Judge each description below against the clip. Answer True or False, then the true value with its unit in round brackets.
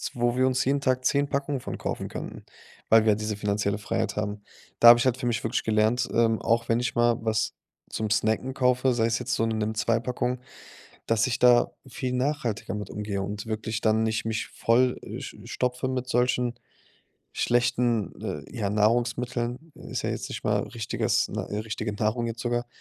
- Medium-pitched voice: False (115 Hz)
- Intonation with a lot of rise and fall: False (2.4 semitones)